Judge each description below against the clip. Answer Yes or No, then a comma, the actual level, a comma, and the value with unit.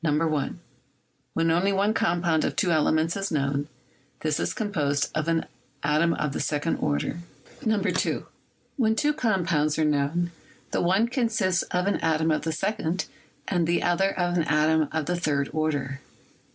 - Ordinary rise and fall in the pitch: Yes, average, 3.5 semitones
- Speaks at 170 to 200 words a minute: No, average, 160 wpm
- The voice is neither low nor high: Yes, medium, 165 Hz